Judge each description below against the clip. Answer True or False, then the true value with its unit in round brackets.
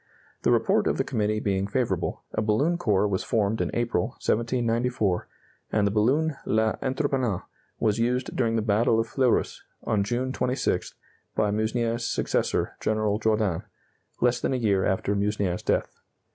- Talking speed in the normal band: True (150 wpm)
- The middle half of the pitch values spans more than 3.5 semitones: False (3.0 semitones)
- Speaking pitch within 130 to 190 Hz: False (110 Hz)